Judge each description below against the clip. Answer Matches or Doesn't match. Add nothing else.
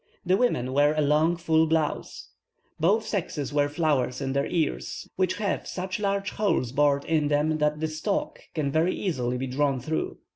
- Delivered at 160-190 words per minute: Matches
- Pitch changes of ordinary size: Matches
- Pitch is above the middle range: Doesn't match